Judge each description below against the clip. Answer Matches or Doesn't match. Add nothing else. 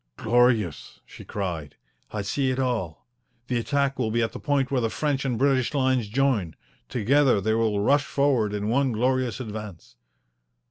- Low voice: Matches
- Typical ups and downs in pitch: Matches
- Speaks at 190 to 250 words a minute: Doesn't match